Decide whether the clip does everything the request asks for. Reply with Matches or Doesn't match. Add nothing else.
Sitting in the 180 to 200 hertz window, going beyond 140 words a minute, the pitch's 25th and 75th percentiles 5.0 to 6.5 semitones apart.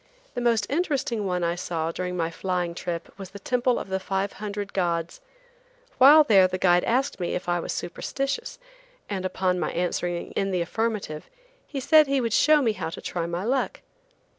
Matches